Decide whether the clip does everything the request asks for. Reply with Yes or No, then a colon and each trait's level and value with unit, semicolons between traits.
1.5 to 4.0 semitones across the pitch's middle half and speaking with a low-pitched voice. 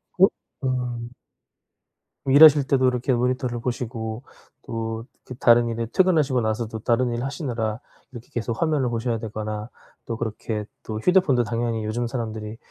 Yes: narrow, 2.4 semitones; low, 120 Hz